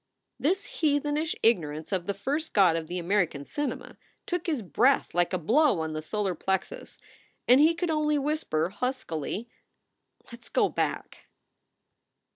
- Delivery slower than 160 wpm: Yes, average, 150 wpm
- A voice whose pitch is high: Yes, high, 225 Hz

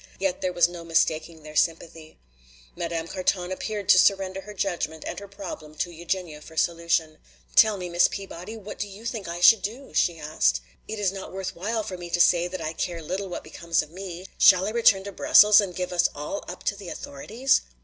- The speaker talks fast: Yes, fast, 215 wpm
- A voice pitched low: No, medium, 180 Hz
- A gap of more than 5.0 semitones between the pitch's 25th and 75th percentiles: No, average, 3.0 semitones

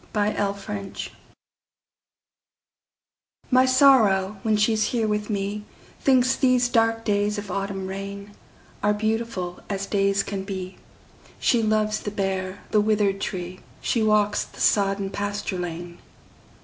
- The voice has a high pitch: Yes, high, 205 Hz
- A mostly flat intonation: Yes, narrow, 1.7 semitones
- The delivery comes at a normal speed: No, slow, 115 wpm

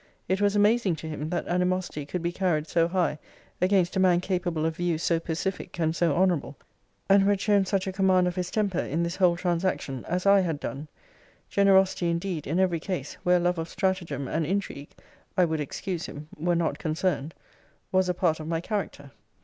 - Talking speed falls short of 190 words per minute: No, average, 200 wpm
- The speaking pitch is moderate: Yes, medium, 175 Hz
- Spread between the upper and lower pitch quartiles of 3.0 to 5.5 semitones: No, narrow, 2.6 semitones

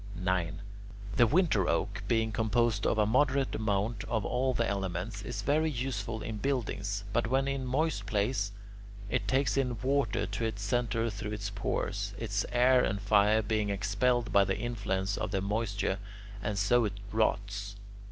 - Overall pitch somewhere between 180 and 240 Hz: No, low, 110 Hz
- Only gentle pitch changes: No, average, 3.4 semitones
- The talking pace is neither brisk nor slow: Yes, average, 170 wpm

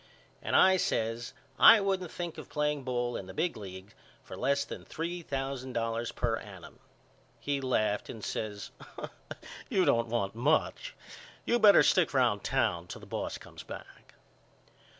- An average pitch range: No, wide, 6.1 semitones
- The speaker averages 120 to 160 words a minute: Yes, average, 155 wpm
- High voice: No, low, 130 Hz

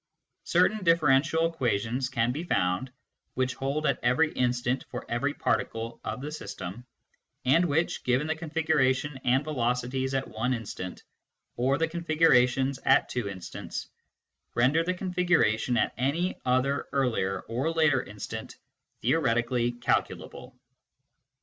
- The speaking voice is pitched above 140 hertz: No, low, 130 Hz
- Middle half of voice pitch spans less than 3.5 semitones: No, average, 4.4 semitones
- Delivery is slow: Yes, slow, 125 wpm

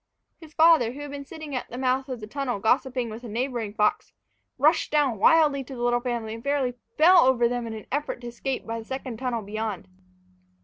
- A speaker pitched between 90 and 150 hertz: No, very high, 250 Hz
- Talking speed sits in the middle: No, fast, 220 wpm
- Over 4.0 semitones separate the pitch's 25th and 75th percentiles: No, average, 3.5 semitones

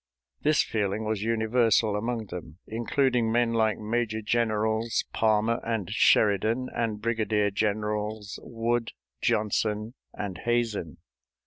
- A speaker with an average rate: No, slow, 110 wpm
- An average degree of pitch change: No, narrow, 1.7 semitones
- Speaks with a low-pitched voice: Yes, low, 110 Hz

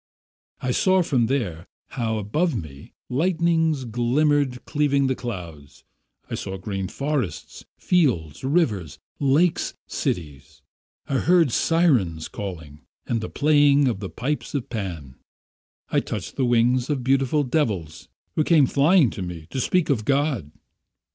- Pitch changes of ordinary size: No, wide, 7.4 semitones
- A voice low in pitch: Yes, low, 125 Hz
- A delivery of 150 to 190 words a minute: No, slow, 135 wpm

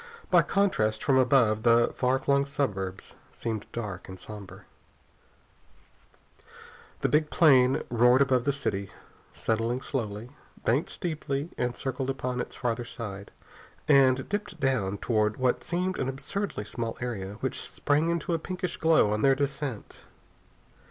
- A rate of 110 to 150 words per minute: Yes, average, 140 wpm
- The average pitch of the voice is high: No, low, 130 Hz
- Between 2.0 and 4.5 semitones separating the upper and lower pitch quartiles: Yes, average, 4.1 semitones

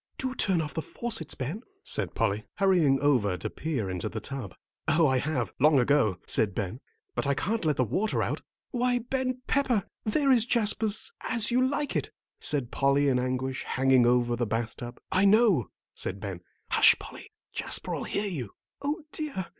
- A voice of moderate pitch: Yes, medium, 145 Hz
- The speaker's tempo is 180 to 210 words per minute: Yes, average, 185 wpm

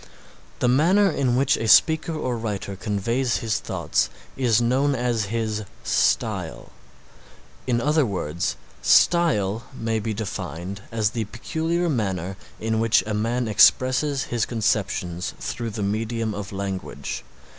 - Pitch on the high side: No, low, 115 Hz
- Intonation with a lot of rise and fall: No, average, 3.8 semitones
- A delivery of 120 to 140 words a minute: Yes, slow, 135 wpm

